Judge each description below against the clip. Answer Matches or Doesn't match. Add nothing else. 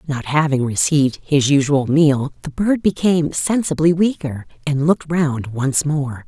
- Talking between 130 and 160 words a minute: Matches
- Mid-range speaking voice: Matches